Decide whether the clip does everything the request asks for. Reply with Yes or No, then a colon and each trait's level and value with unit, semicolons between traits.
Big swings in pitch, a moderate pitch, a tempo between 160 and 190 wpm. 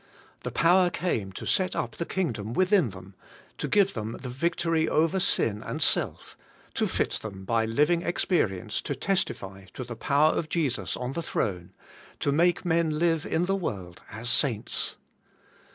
Yes: wide, 7.8 semitones; medium, 150 Hz; average, 170 wpm